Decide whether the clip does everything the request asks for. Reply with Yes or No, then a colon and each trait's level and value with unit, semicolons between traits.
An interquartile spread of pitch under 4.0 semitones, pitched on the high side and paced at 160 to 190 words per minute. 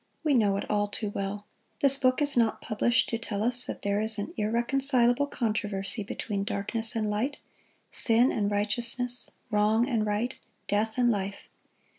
Yes: average, 2.9 semitones; high, 220 Hz; average, 165 wpm